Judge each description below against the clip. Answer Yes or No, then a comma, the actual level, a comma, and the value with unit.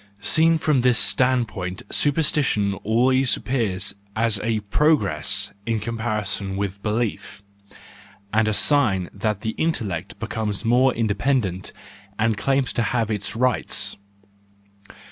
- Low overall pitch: Yes, low, 110 Hz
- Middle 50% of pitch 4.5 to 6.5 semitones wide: No, average, 4.0 semitones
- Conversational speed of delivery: No, slow, 125 wpm